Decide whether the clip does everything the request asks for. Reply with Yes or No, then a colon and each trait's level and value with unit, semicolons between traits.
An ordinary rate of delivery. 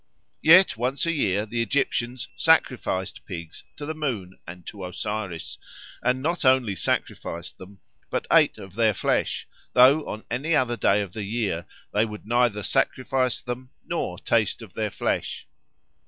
Yes: average, 155 wpm